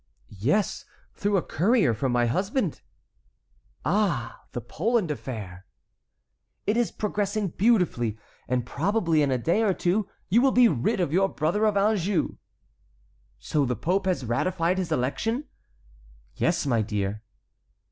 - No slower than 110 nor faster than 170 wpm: Yes, slow, 135 wpm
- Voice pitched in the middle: Yes, medium, 175 Hz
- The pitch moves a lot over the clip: Yes, wide, 8.5 semitones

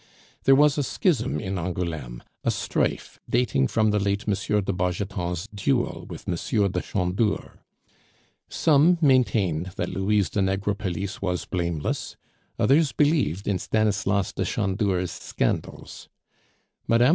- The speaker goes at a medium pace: No, slow, 125 wpm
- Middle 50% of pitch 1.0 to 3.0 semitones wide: No, average, 4.2 semitones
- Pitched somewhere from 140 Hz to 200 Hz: No, low, 100 Hz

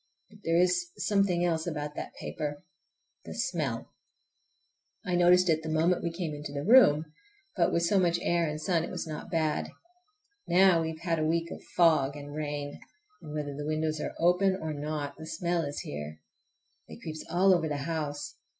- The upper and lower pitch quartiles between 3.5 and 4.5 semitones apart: No, average, 2.7 semitones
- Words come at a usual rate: Yes, average, 185 wpm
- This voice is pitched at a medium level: Yes, medium, 160 Hz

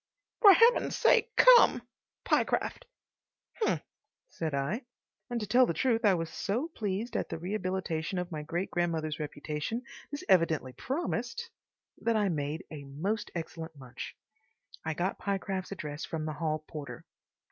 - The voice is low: No, medium, 180 Hz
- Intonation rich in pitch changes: Yes, wide, 6.6 semitones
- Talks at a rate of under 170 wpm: Yes, average, 145 wpm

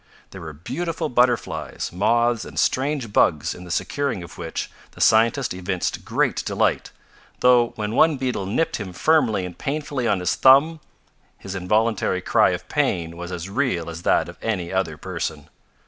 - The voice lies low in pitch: Yes, low, 105 Hz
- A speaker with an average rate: Yes, average, 165 wpm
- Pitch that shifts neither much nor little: No, wide, 6.3 semitones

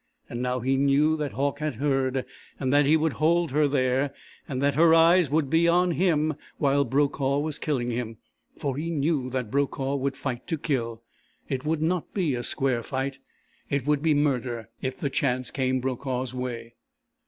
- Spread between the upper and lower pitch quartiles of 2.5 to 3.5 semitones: Yes, average, 2.9 semitones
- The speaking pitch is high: No, medium, 140 Hz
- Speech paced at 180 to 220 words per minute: Yes, average, 190 wpm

